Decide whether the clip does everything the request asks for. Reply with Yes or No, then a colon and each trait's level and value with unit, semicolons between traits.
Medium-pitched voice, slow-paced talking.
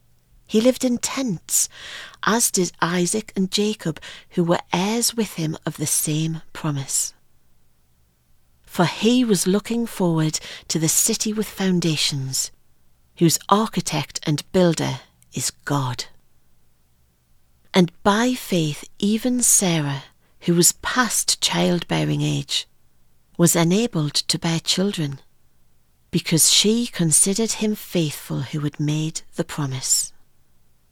Yes: medium, 160 Hz; slow, 115 wpm